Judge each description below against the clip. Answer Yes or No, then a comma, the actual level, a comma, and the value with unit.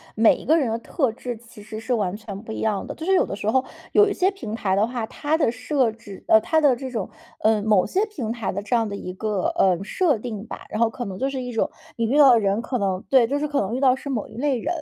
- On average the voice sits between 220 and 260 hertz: Yes, high, 230 Hz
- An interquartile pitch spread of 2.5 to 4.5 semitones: Yes, average, 4.1 semitones